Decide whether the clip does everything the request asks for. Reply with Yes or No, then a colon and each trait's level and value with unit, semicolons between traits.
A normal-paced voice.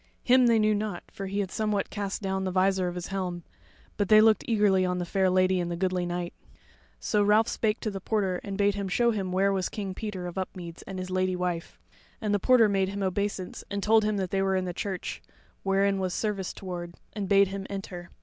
No: fast, 235 wpm